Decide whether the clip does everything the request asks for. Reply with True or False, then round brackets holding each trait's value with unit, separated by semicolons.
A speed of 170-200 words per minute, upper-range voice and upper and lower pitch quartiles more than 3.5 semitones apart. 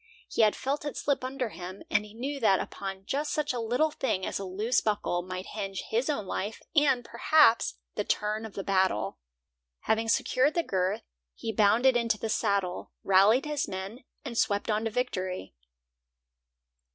True (175 wpm; 220 Hz; 4.7 semitones)